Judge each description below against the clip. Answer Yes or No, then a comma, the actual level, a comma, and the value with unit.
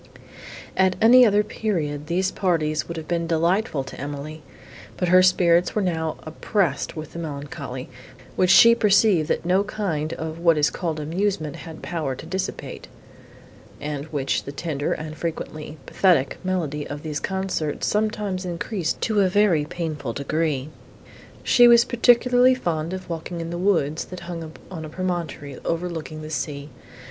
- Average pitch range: Yes, average, 3.6 semitones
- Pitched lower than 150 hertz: No, medium, 165 Hz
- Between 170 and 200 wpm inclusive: No, average, 155 wpm